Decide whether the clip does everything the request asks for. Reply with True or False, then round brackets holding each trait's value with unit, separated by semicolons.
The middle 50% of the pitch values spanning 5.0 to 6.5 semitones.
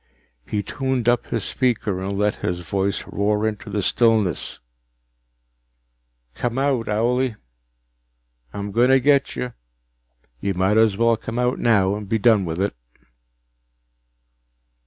False (3.5 semitones)